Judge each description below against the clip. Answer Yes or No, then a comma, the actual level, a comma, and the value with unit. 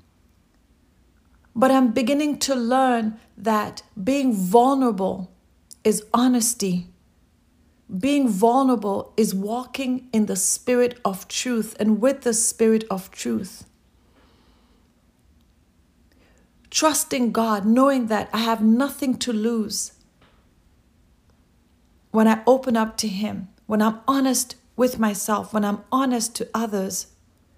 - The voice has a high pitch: Yes, high, 225 Hz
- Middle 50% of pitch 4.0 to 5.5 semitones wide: No, average, 3.6 semitones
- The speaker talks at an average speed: No, slow, 110 wpm